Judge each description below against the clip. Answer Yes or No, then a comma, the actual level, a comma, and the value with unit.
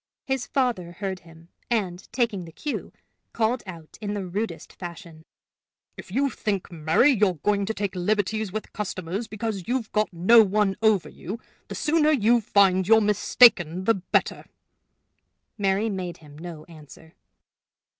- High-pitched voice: Yes, high, 200 Hz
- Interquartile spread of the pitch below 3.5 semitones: No, average, 4.0 semitones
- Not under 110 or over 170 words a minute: Yes, average, 150 wpm